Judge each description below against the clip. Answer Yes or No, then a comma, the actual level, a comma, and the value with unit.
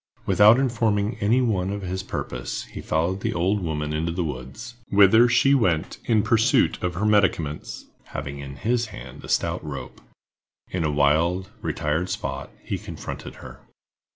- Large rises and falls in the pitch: Yes, wide, 6.1 semitones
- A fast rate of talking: No, average, 155 wpm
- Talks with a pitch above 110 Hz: No, very low, 95 Hz